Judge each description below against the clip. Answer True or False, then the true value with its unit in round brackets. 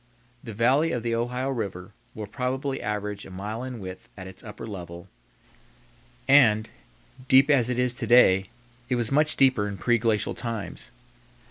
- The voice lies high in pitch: False (115 Hz)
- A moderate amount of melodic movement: True (3.7 semitones)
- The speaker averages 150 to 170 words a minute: True (160 wpm)